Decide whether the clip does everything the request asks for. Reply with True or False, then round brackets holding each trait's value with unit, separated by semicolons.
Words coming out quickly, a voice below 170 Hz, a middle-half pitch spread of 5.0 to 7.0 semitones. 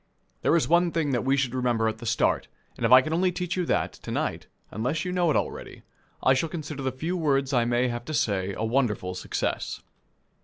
True (230 wpm; 135 Hz; 5.3 semitones)